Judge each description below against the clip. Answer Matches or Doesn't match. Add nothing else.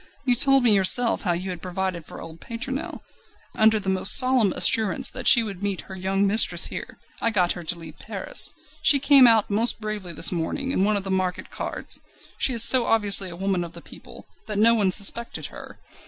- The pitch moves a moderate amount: Matches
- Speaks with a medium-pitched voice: Doesn't match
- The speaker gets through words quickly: Matches